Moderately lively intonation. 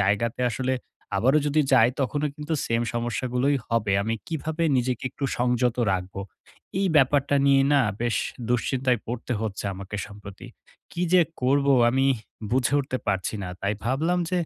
Yes: average, 3.7 semitones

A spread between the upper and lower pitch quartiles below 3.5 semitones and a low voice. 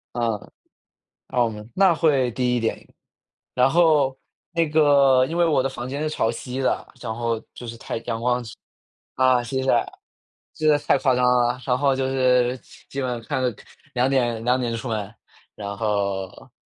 Yes: narrow, 2.4 semitones; low, 125 Hz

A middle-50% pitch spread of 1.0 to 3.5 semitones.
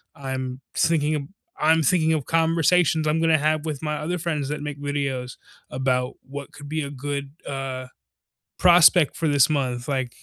Yes: average, 2.8 semitones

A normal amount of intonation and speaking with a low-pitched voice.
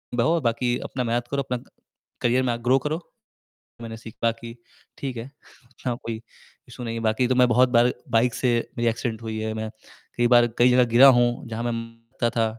No: narrow, 1.5 semitones; low, 120 Hz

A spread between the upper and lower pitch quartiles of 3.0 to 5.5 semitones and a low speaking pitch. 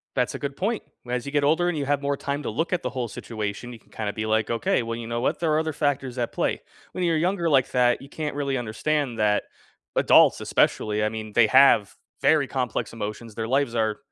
Yes: average, 4.5 semitones; low, 125 Hz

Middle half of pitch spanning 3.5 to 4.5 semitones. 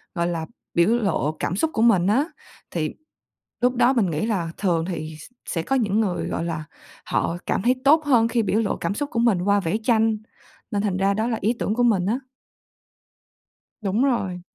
No: average, 4.9 semitones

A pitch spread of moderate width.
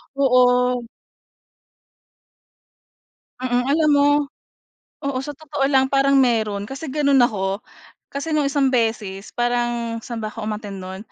Yes: average, 3.7 semitones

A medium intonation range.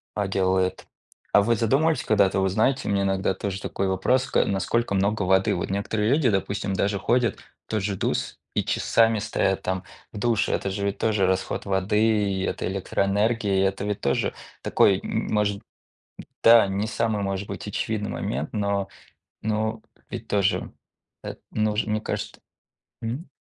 No: narrow, 2.2 semitones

